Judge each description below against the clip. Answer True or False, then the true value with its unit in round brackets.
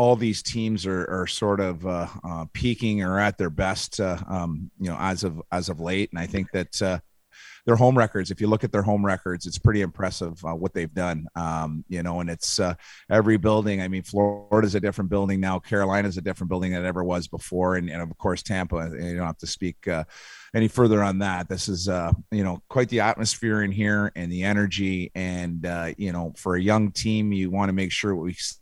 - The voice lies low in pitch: True (95 Hz)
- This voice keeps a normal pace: False (240 wpm)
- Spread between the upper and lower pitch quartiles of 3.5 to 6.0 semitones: False (2.7 semitones)